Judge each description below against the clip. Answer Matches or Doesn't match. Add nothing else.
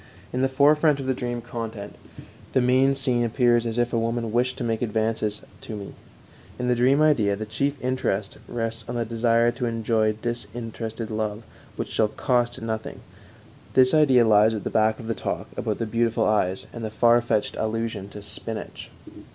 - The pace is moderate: Matches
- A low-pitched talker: Matches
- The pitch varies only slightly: Matches